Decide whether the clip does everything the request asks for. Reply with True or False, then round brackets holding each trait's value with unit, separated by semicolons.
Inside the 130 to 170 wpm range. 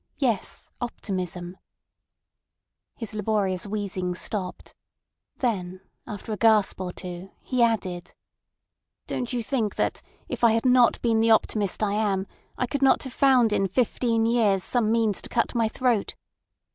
True (145 wpm)